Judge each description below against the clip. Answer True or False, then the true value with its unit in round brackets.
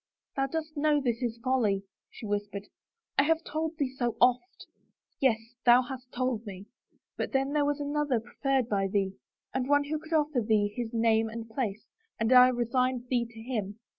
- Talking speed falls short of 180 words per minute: False (195 wpm)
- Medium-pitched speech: False (250 Hz)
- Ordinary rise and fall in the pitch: True (4.1 semitones)